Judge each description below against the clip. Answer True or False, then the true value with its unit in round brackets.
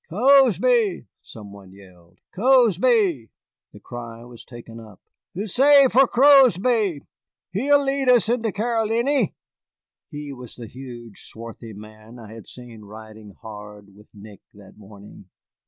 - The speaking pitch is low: True (125 Hz)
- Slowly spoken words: True (125 wpm)